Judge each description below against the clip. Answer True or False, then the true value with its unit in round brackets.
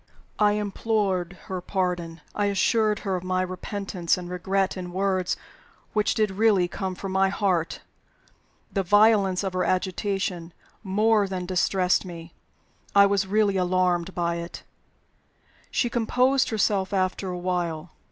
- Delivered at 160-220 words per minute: False (140 wpm)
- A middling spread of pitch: False (2.1 semitones)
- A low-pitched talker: False (190 Hz)